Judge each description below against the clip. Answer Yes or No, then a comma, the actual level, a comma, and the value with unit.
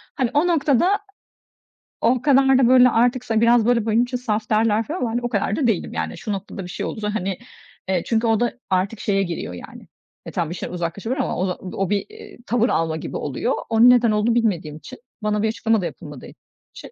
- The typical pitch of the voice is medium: No, high, 225 Hz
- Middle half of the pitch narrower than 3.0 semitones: No, average, 4.0 semitones